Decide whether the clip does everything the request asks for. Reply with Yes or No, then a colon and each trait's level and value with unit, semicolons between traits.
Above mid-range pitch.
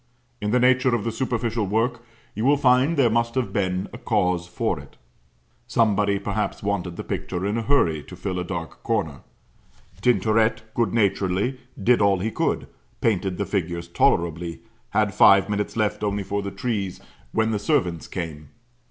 No: low, 105 Hz